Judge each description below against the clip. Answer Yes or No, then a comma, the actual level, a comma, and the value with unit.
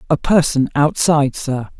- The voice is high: No, medium, 145 Hz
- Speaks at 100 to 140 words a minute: Yes, slow, 135 wpm